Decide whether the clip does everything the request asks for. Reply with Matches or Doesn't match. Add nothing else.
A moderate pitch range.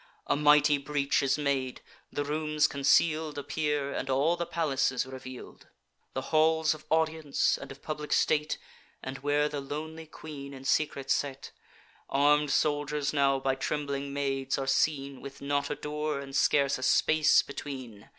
Doesn't match